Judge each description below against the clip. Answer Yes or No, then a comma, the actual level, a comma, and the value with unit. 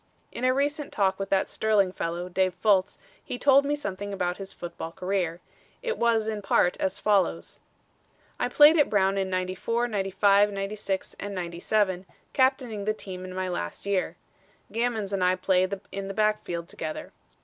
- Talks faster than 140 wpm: Yes, average, 170 wpm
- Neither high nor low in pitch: No, high, 195 Hz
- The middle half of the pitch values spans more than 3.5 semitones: No, average, 2.8 semitones